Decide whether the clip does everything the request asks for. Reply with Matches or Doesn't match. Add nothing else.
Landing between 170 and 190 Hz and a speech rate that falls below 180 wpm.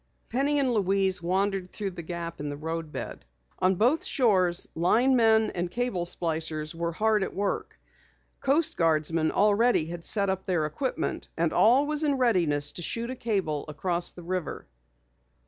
Matches